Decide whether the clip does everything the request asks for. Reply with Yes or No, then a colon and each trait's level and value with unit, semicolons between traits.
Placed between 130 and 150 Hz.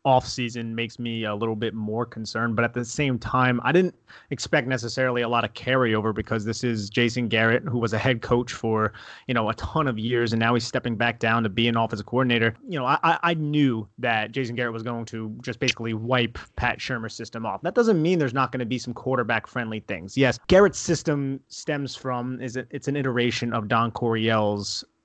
No: low, 120 Hz